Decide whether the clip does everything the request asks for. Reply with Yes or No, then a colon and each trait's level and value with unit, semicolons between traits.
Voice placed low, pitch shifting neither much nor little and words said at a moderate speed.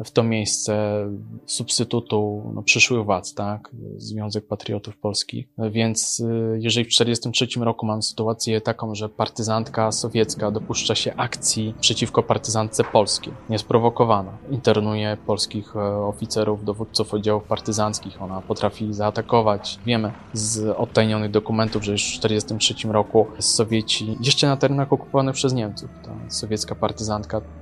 No: low, 110 Hz; narrow, 1.5 semitones; average, 125 wpm